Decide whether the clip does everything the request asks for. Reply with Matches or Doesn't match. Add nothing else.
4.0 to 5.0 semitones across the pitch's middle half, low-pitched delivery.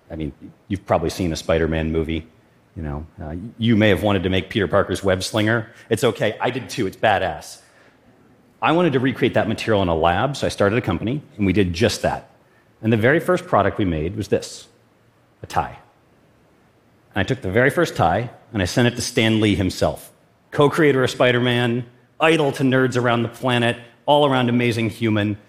Matches